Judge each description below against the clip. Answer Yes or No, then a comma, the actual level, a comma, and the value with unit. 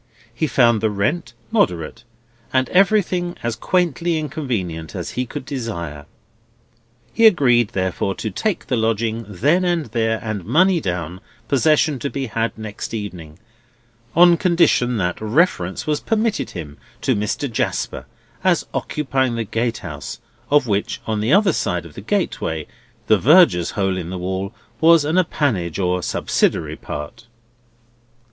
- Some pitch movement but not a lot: No, wide, 8.2 semitones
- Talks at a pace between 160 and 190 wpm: No, average, 145 wpm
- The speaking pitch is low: Yes, low, 115 Hz